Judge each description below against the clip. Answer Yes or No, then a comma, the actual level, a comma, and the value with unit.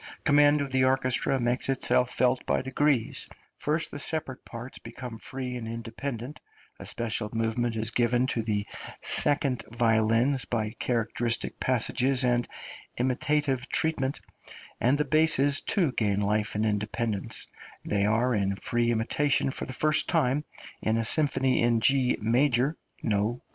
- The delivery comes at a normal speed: Yes, average, 145 wpm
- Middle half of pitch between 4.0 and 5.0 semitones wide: No, average, 3.2 semitones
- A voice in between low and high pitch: No, low, 125 Hz